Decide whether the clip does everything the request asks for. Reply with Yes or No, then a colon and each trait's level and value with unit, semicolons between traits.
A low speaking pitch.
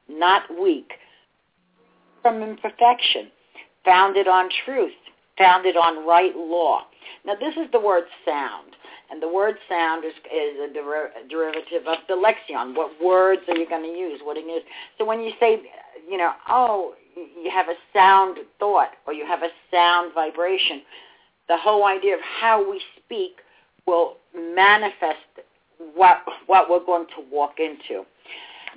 No: medium, 185 Hz